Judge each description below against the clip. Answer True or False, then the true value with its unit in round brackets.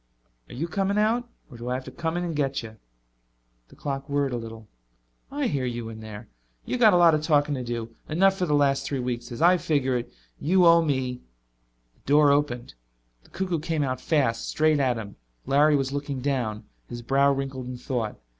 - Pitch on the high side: False (140 Hz)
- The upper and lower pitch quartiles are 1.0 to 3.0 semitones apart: False (4.4 semitones)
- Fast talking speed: True (215 wpm)